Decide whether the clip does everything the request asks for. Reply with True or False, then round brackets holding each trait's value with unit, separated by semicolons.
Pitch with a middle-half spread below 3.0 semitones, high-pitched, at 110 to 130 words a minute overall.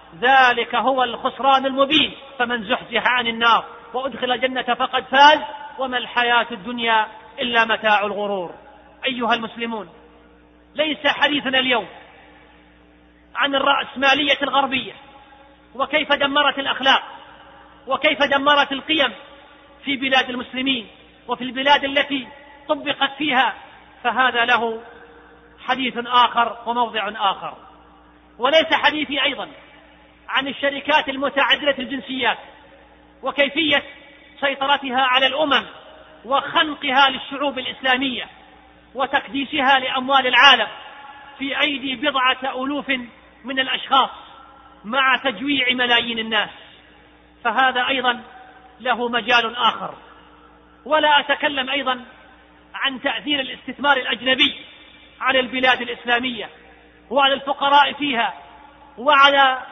False (2.6 semitones; 265 Hz; 90 wpm)